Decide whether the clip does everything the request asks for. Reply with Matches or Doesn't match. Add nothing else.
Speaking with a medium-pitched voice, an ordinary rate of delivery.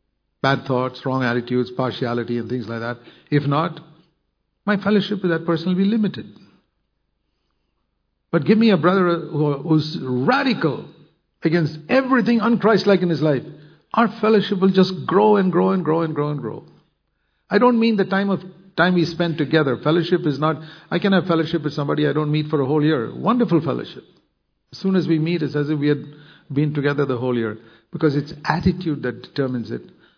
Matches